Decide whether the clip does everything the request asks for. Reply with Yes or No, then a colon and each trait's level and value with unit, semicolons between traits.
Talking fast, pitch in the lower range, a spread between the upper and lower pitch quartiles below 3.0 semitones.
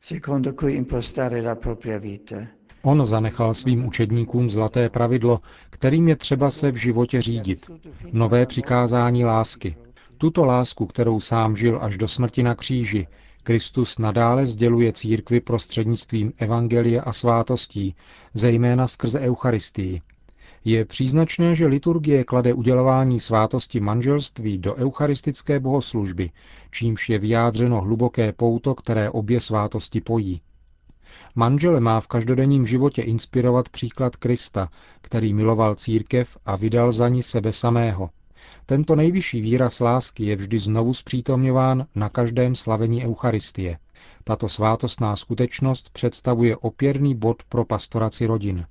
No: slow, 115 wpm; low, 120 Hz; narrow, 2.4 semitones